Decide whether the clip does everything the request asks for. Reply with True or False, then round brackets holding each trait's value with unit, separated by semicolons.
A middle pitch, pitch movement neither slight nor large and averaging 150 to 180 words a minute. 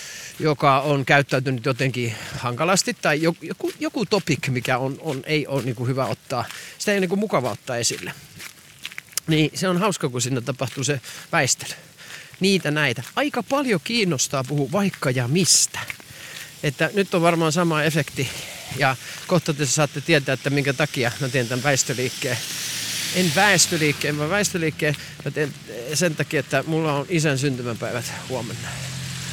True (150 Hz; 4.1 semitones; 155 wpm)